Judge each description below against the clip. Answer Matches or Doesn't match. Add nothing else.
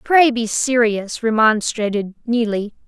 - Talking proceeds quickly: Doesn't match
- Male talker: Doesn't match